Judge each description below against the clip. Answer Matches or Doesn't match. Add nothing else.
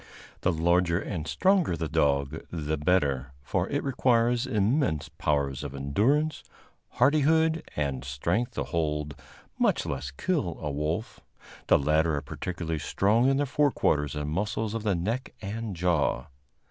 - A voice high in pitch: Doesn't match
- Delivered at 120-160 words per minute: Matches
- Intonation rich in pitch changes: Matches